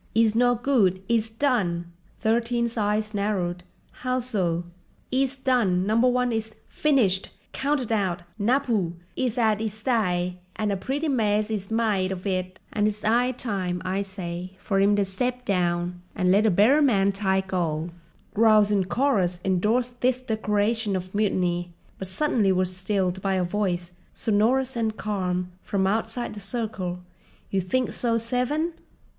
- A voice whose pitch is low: No, high, 210 Hz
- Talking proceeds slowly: No, average, 150 wpm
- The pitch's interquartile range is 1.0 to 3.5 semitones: No, average, 4.1 semitones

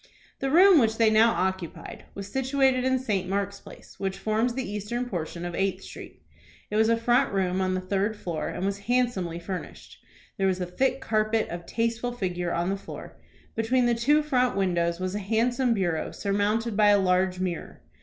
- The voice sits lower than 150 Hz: No, high, 205 Hz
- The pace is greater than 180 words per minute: Yes, average, 195 wpm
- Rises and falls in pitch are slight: No, average, 4.3 semitones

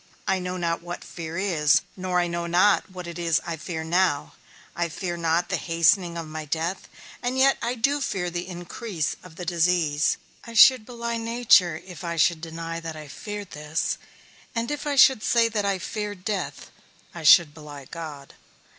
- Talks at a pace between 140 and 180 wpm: No, average, 190 wpm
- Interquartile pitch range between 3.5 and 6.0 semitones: Yes, average, 3.9 semitones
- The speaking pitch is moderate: Yes, medium, 175 Hz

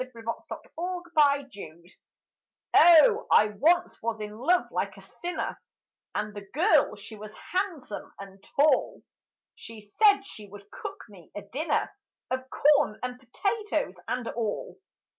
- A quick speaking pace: No, average, 140 wpm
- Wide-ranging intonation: Yes, wide, 8.0 semitones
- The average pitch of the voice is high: Yes, very high, 250 Hz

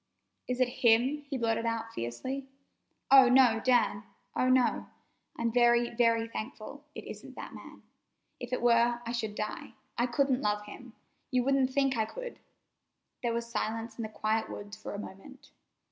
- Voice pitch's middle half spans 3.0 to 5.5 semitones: No, narrow, 2.4 semitones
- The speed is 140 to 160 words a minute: No, average, 170 wpm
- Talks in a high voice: Yes, high, 235 Hz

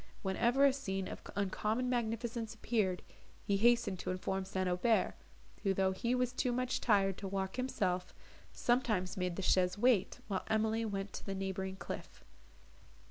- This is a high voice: Yes, high, 200 Hz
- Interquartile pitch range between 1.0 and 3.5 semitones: No, average, 3.9 semitones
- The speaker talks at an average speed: Yes, average, 160 wpm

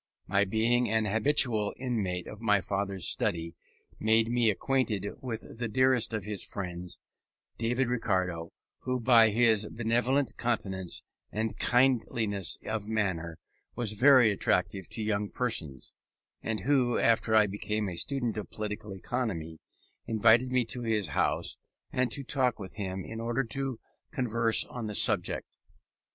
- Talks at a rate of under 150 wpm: Yes, average, 140 wpm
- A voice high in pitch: No, low, 110 Hz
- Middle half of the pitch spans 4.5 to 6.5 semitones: No, average, 3.2 semitones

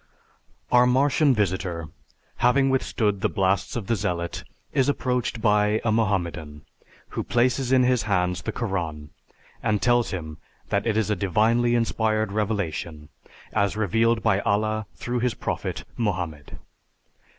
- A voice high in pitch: No, low, 110 Hz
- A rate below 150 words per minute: Yes, average, 140 wpm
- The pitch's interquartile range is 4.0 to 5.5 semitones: Yes, average, 4.4 semitones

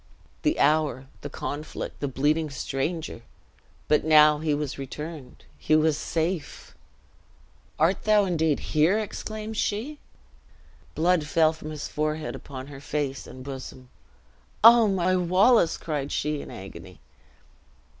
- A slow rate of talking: Yes, slow, 125 wpm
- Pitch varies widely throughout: No, average, 3.8 semitones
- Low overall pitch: No, medium, 155 Hz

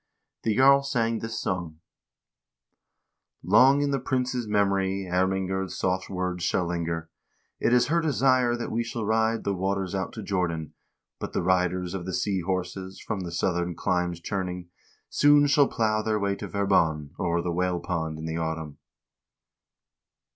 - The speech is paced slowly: No, average, 160 wpm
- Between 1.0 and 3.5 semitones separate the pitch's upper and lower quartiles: No, average, 4.3 semitones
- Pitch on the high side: No, very low, 95 Hz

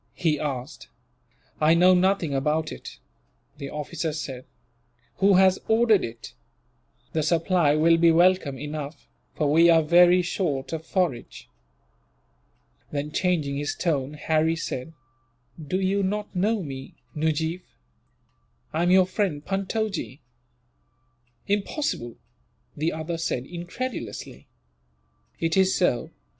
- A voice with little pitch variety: No, average, 3.8 semitones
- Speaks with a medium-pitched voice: Yes, medium, 165 Hz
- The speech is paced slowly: Yes, slow, 120 wpm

